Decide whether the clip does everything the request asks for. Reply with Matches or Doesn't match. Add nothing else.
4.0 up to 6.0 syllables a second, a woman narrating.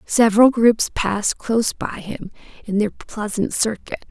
Matches